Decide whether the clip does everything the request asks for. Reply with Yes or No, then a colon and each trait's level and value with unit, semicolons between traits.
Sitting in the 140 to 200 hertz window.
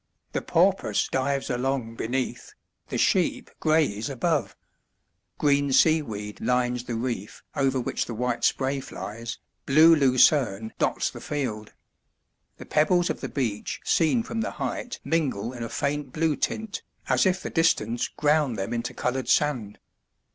No: low, 130 Hz